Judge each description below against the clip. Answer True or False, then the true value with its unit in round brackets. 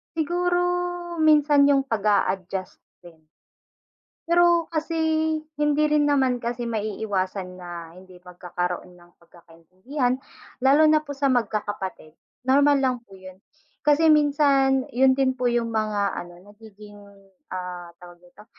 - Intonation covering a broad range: True (7.6 semitones)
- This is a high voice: True (225 Hz)